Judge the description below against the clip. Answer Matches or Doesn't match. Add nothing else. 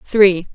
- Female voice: Matches